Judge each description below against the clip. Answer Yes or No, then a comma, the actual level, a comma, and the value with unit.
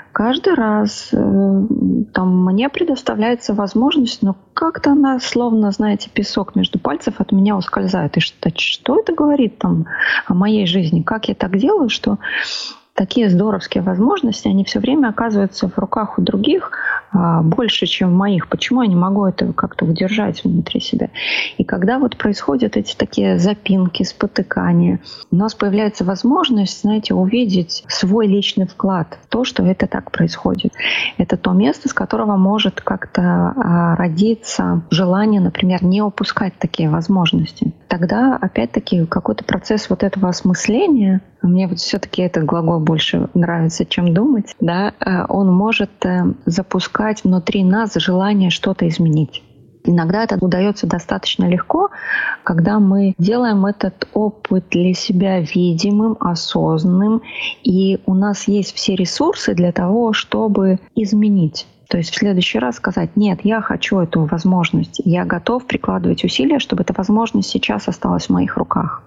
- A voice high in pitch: Yes, high, 200 Hz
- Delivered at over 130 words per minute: Yes, average, 140 wpm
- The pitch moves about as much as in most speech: Yes, average, 3.4 semitones